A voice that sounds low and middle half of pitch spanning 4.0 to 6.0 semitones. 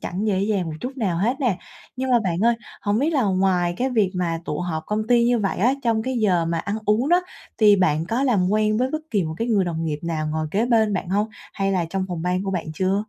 No: high, 200 Hz; average, 4.5 semitones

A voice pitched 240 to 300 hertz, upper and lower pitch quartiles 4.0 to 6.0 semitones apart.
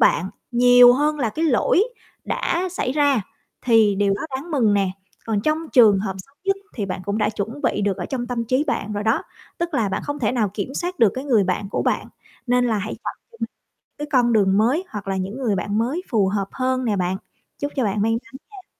No: high, 230 Hz; average, 4.7 semitones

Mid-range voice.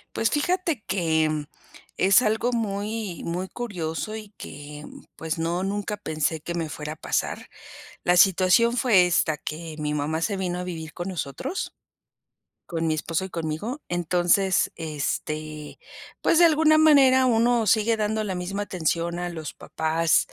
Yes: medium, 180 Hz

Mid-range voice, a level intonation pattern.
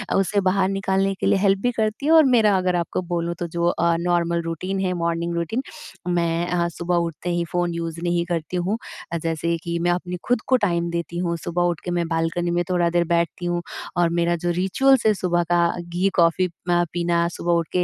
Yes: medium, 175 Hz; narrow, 1.4 semitones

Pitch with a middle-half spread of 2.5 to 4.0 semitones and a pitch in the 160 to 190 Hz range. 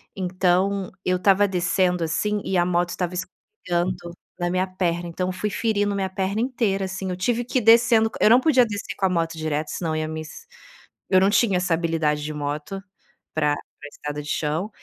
Yes: average, 3.4 semitones; medium, 185 Hz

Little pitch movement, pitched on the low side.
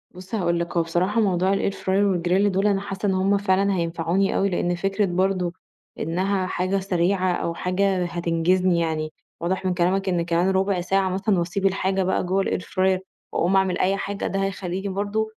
No: narrow, 1.8 semitones; medium, 185 Hz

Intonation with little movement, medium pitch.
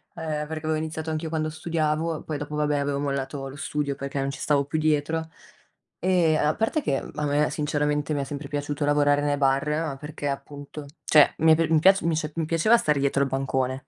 Yes: narrow, 1.9 semitones; medium, 150 Hz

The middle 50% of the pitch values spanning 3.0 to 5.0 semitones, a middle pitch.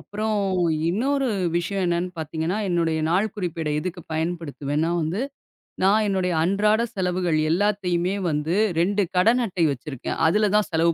Yes: average, 3.8 semitones; medium, 180 Hz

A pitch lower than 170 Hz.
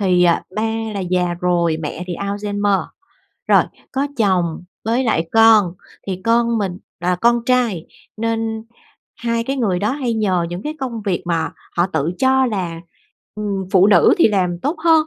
No: high, 205 Hz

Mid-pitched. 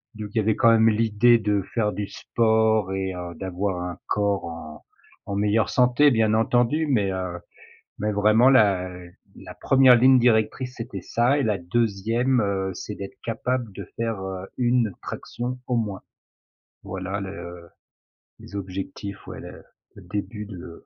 No: low, 105 Hz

